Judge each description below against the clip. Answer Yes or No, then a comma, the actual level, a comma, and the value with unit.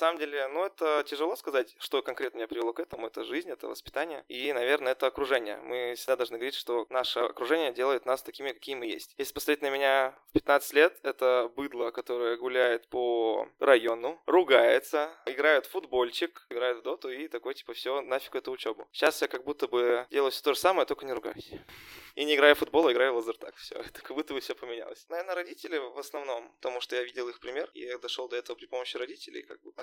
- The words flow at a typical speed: No, fast, 220 wpm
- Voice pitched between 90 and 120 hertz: No, medium, 140 Hz